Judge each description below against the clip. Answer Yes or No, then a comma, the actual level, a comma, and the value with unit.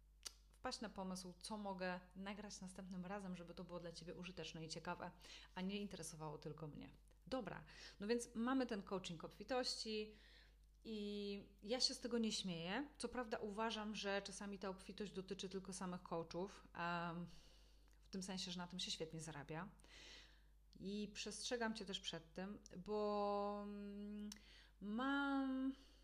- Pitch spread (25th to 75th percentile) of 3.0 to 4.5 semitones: Yes, average, 3.3 semitones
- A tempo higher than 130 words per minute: Yes, average, 145 wpm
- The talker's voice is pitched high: Yes, high, 200 Hz